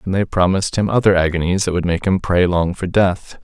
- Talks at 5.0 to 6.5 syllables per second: Yes, 5.7 syllables/s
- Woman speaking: No, male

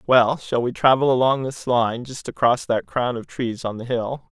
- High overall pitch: No, low, 120 Hz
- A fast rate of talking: Yes, fast, 220 wpm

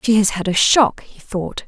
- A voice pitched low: No, high, 205 Hz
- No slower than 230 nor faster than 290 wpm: Yes, fast, 250 wpm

